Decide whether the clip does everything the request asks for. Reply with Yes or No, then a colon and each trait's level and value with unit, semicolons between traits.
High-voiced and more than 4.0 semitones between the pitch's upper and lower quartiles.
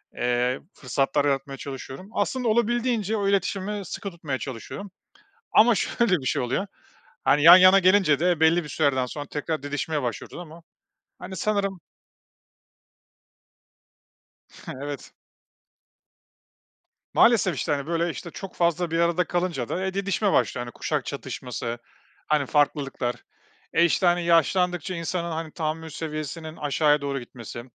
No: medium, 165 Hz; average, 4.7 semitones